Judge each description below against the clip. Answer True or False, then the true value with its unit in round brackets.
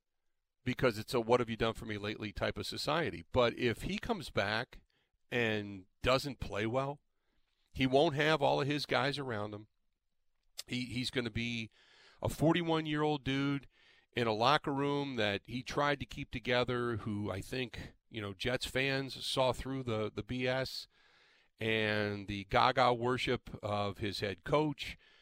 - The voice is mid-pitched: False (125 Hz)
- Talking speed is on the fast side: False (170 wpm)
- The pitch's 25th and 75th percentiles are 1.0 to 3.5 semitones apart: False (4.3 semitones)